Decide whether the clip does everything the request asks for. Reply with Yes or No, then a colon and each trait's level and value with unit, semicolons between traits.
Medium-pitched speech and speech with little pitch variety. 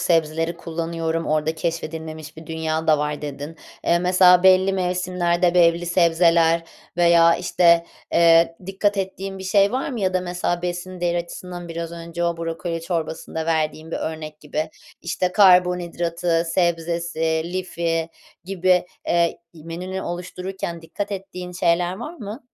Yes: medium, 170 Hz; narrow, 1.6 semitones